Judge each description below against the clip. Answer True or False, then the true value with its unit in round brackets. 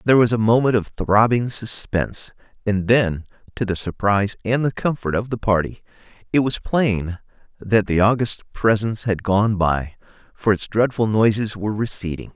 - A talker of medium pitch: False (105 Hz)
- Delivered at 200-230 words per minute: False (165 wpm)